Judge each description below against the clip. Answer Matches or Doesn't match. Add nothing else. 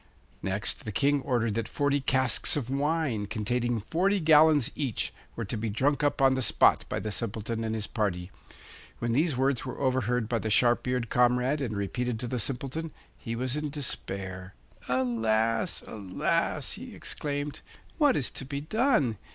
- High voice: Doesn't match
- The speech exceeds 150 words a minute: Matches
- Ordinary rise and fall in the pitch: Matches